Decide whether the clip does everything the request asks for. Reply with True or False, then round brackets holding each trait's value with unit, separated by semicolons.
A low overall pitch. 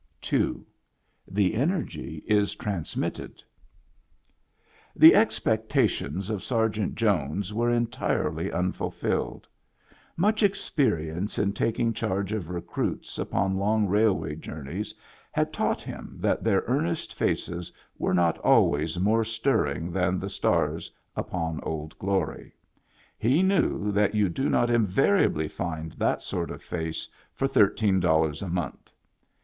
True (100 Hz)